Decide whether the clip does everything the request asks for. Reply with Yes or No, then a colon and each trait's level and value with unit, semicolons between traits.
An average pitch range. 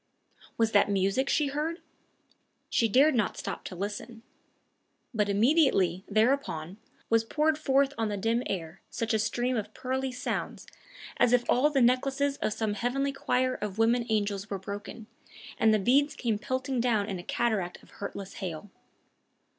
Yes: average, 4.4 semitones